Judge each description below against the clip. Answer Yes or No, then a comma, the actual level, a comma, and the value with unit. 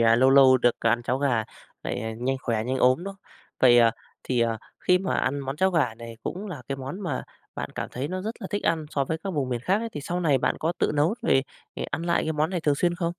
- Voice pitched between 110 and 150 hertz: Yes, medium, 140 Hz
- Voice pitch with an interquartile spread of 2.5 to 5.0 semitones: No, wide, 5.6 semitones